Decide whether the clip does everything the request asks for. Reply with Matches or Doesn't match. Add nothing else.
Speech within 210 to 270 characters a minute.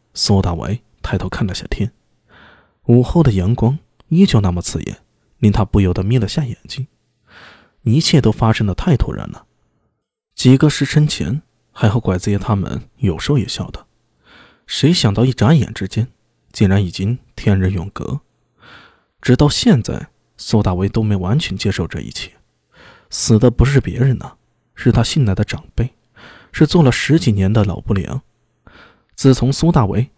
Matches